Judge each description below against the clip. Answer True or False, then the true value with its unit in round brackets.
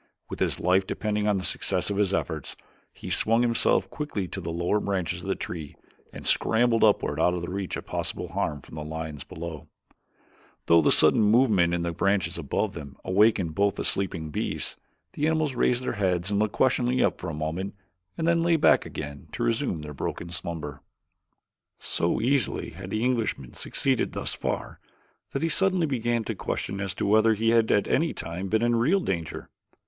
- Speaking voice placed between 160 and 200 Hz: False (100 Hz)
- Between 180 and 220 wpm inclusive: True (195 wpm)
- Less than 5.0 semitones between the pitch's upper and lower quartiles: False (5.6 semitones)